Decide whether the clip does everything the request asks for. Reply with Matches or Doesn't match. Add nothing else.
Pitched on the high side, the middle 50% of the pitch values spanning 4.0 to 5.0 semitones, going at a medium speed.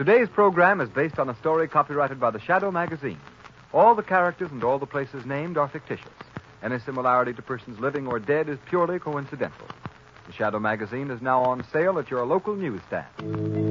Doesn't match